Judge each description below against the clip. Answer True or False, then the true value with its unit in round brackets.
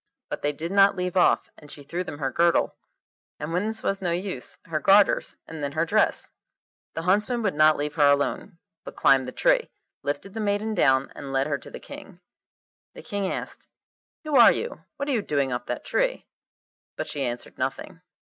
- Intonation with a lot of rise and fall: True (5.8 semitones)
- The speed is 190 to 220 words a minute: True (205 wpm)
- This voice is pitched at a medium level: True (170 Hz)